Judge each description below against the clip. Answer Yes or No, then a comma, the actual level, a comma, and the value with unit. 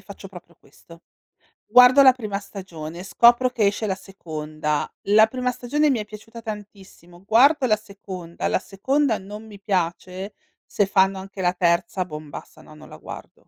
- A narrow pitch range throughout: No, average, 4.0 semitones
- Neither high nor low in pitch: No, high, 200 Hz